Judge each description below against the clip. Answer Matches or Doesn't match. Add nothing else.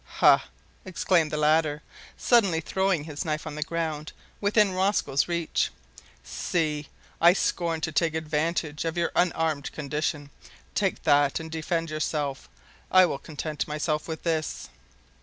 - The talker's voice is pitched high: Doesn't match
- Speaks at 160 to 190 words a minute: Doesn't match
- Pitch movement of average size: Doesn't match